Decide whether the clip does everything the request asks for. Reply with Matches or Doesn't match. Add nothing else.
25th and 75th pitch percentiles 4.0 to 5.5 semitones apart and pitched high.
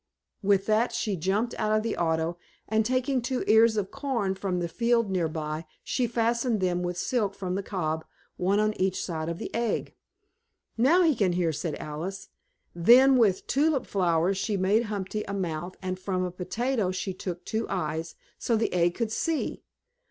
Matches